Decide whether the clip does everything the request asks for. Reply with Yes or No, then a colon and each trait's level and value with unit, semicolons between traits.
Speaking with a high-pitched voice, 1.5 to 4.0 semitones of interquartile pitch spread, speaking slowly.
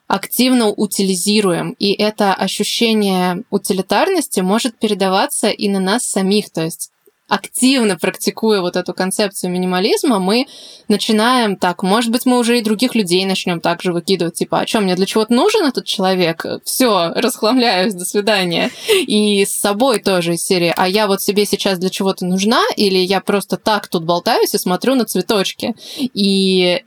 No: high, 205 Hz; average, 3.4 semitones; fast, 160 wpm